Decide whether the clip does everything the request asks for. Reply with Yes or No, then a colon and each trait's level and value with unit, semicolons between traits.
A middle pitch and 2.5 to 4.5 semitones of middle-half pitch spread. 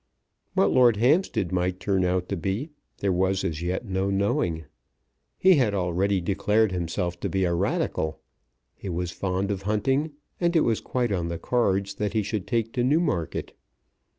No: very low, 95 Hz; average, 4.0 semitones